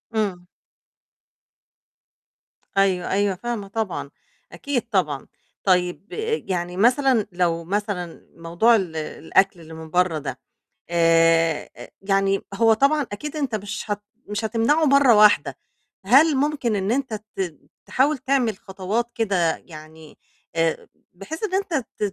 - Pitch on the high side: Yes, high, 200 Hz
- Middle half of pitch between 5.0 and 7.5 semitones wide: Yes, wide, 5.4 semitones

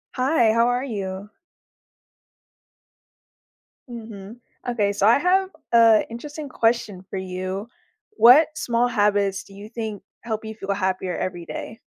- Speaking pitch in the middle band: No, high, 220 Hz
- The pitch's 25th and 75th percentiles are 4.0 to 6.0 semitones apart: No, average, 3.4 semitones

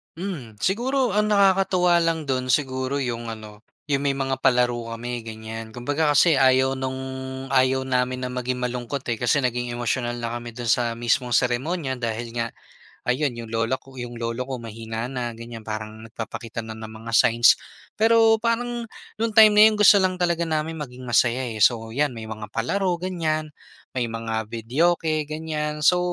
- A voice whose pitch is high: No, low, 130 Hz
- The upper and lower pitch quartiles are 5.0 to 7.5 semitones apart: Yes, average, 5.3 semitones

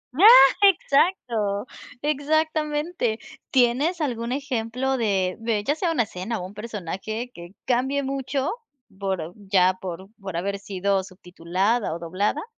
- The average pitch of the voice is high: Yes, high, 225 Hz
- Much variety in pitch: Yes, wide, 6.3 semitones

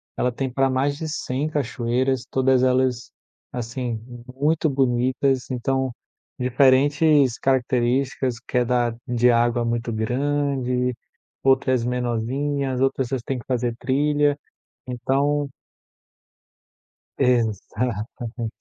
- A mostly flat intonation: Yes, narrow, 2.0 semitones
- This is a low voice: Yes, low, 130 Hz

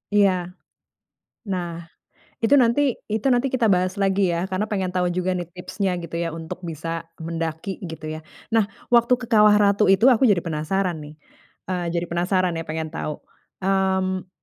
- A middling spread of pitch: Yes, average, 3.1 semitones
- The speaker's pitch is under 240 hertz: Yes, medium, 185 Hz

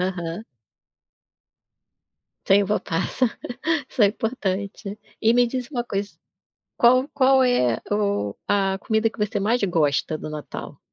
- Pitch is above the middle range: Yes, high, 205 Hz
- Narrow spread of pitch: No, average, 4.1 semitones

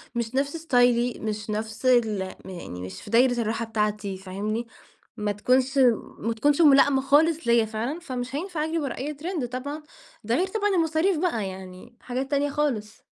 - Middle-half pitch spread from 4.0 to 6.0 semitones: Yes, average, 5.2 semitones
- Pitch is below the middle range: No, high, 245 Hz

